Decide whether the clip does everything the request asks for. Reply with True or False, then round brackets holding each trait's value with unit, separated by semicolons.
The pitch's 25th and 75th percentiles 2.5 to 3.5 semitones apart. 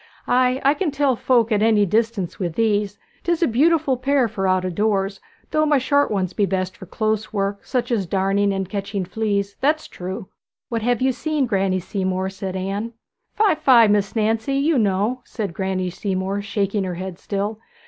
False (4.3 semitones)